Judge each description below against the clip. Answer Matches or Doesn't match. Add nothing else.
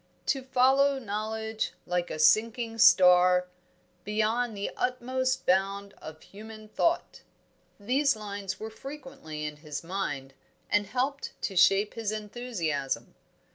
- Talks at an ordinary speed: Doesn't match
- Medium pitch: Doesn't match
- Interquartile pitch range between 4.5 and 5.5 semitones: Matches